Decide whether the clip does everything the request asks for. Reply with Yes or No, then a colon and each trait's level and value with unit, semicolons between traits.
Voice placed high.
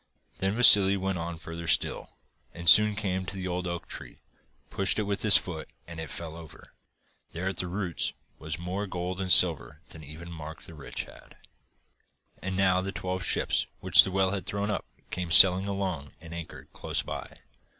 No: very low, 90 Hz